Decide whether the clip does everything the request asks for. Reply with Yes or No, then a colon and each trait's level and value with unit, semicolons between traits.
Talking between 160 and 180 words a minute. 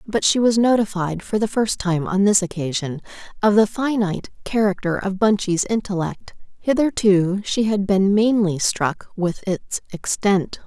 No: average, 150 wpm